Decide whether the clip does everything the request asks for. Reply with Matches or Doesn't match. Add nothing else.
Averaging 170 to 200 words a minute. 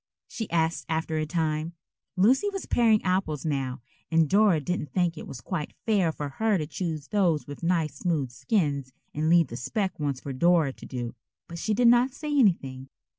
Matches